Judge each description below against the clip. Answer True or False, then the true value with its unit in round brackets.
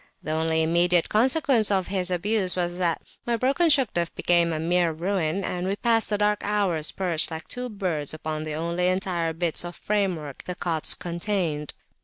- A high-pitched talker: False (180 Hz)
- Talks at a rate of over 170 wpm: True (180 wpm)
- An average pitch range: True (3.9 semitones)